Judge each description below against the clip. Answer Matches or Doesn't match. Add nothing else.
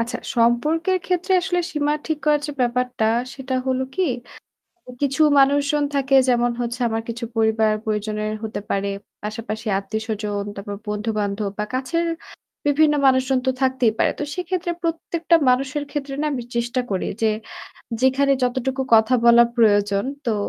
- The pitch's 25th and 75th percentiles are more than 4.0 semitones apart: Matches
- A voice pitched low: Doesn't match